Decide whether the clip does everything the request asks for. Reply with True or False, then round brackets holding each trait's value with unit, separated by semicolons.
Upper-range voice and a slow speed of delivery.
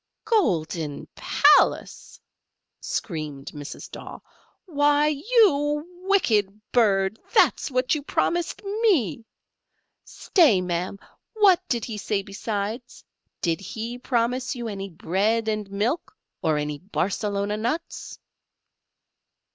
True (225 Hz; 100 wpm)